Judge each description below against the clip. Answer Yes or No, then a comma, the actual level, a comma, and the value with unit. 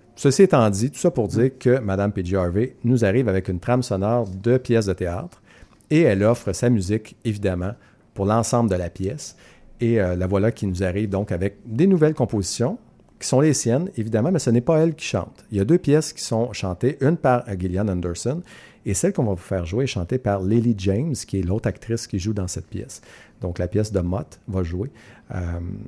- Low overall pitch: Yes, low, 110 Hz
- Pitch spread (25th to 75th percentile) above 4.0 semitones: Yes, average, 4.4 semitones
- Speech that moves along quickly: Yes, fast, 225 wpm